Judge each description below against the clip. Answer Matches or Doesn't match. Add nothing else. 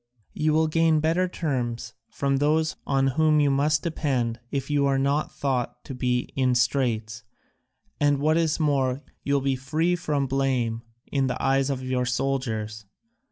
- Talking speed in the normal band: Matches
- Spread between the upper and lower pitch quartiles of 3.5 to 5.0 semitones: Doesn't match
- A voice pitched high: Doesn't match